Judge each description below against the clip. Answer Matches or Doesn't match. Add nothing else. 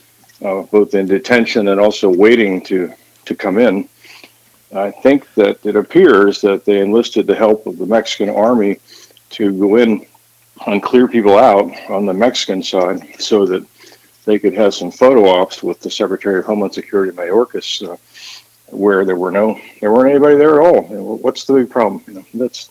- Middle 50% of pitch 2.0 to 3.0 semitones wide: Doesn't match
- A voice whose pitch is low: Matches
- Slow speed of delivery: Doesn't match